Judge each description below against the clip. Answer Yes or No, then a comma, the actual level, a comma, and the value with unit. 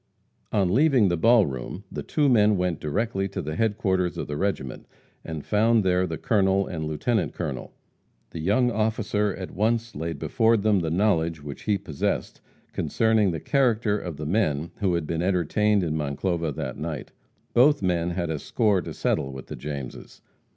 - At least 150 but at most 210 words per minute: Yes, average, 180 wpm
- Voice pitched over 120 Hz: No, very low, 95 Hz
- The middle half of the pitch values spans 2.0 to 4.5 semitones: No, average, 5.0 semitones